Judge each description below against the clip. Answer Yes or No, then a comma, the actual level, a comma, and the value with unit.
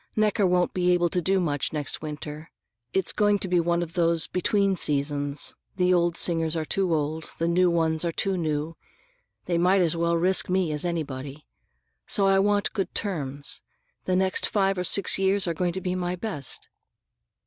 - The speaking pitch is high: No, medium, 175 Hz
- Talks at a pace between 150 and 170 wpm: No, average, 190 wpm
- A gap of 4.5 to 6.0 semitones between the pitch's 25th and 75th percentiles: No, average, 3.0 semitones